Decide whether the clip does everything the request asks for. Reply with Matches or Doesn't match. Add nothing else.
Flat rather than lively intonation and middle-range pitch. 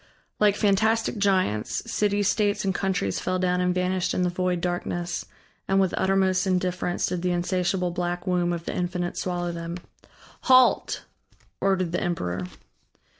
Matches